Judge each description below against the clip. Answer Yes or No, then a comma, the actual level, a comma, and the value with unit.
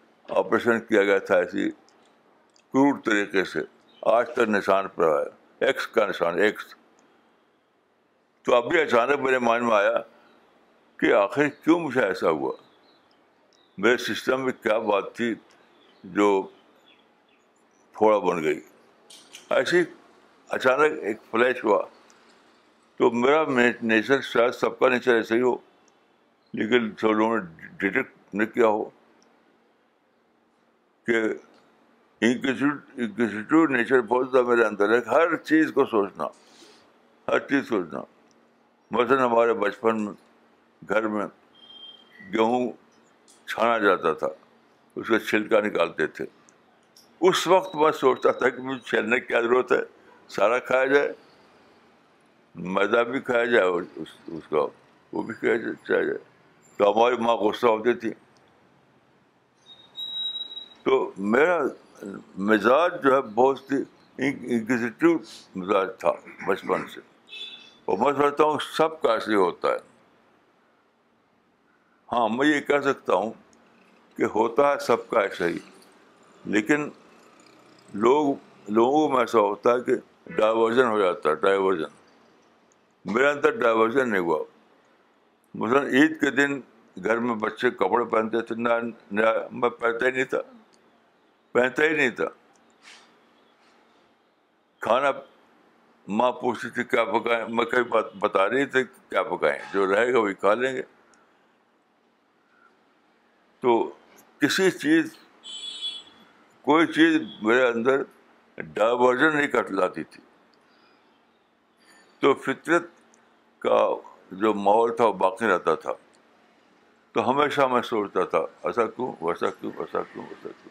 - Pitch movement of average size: No, wide, 5.8 semitones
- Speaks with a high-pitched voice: No, low, 130 Hz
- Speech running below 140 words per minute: Yes, average, 125 wpm